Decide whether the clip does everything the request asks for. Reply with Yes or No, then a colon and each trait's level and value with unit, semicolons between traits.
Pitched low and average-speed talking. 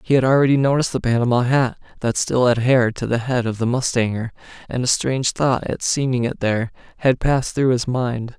No: low, 125 Hz; fast, 210 wpm